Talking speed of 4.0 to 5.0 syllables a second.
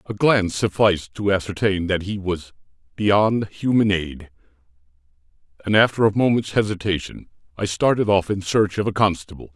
No: 5.2 syllables/s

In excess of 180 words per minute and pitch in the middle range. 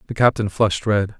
No: average, 200 wpm; low, 100 Hz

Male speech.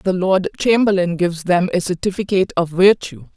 No: female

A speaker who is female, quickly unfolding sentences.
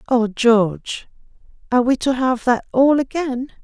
No: female; average, 150 wpm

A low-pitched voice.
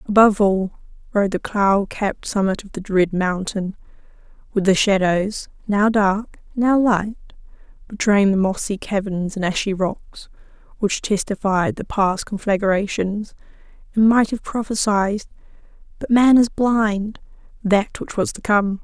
No: high, 205 Hz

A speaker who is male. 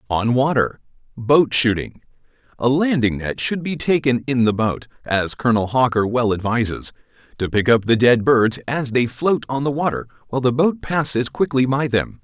Yes: male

